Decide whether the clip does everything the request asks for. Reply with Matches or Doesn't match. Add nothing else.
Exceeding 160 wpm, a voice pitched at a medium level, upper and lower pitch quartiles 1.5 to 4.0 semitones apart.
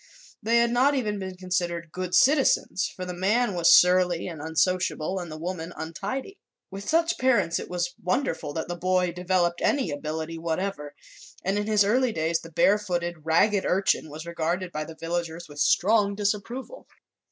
Matches